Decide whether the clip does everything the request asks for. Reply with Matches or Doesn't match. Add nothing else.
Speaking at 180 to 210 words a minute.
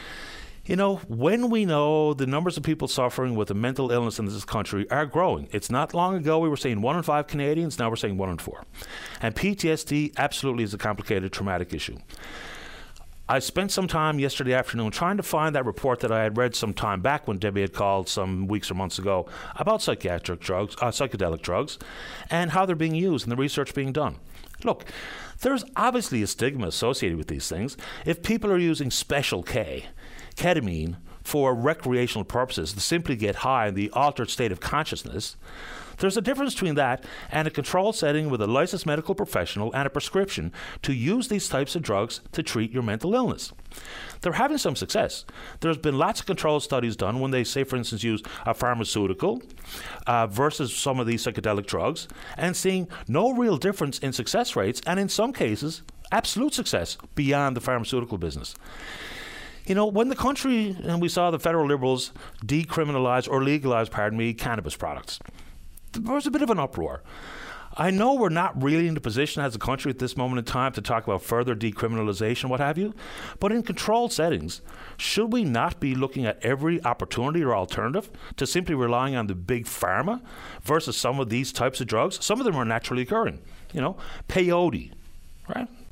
Matches